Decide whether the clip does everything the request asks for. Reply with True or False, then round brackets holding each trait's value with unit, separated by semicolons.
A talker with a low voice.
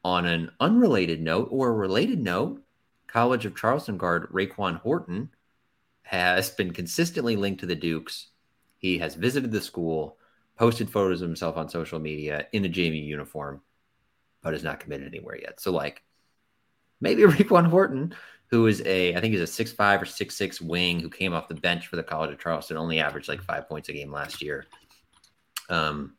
True (90 Hz)